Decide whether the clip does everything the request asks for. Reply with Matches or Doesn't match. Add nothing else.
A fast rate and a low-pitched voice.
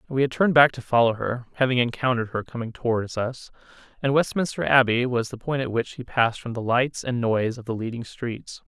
Matches